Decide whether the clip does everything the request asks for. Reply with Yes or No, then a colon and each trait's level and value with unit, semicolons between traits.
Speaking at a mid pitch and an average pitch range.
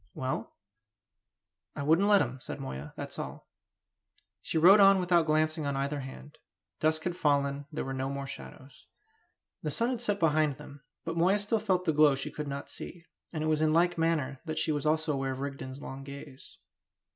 Yes: medium, 150 Hz; average, 3.4 semitones